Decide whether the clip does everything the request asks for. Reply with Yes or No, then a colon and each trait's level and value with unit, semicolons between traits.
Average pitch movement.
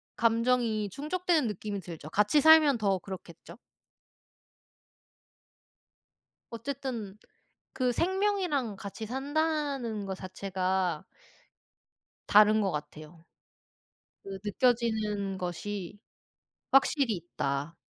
No: wide, 5.9 semitones